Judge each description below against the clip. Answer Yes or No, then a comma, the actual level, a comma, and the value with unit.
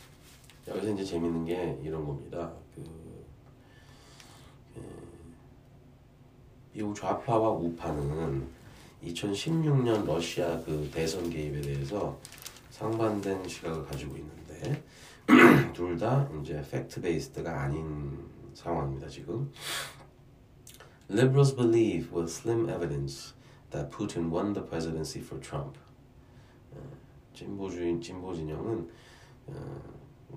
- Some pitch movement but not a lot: No, wide, 6.7 semitones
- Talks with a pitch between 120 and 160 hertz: No, very low, 85 Hz